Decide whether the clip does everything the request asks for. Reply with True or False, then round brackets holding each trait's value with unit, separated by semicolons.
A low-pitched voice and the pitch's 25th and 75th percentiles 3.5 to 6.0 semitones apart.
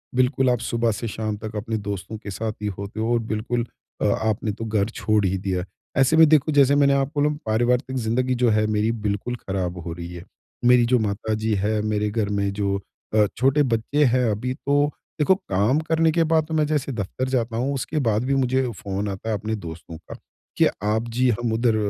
True (115 Hz; 4.0 semitones)